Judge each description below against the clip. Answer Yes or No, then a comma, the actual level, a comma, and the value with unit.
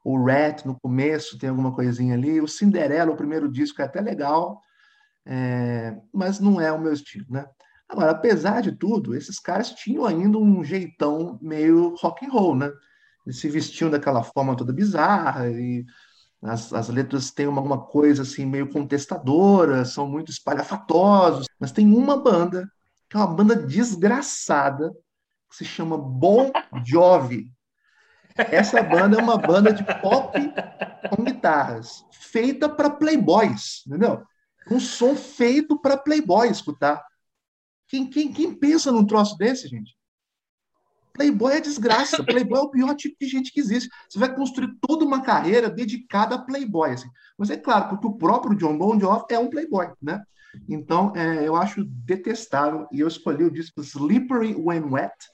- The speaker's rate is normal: Yes, average, 160 wpm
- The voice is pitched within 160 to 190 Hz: Yes, medium, 185 Hz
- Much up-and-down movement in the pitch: Yes, wide, 8.5 semitones